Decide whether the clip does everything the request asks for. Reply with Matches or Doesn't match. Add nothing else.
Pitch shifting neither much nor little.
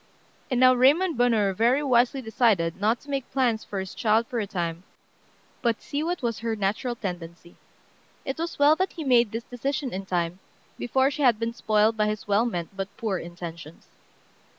Matches